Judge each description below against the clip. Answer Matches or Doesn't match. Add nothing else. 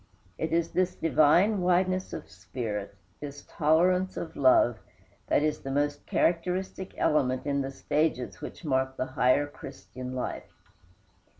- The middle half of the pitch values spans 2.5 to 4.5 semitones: Doesn't match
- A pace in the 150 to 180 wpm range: Doesn't match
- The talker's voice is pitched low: Doesn't match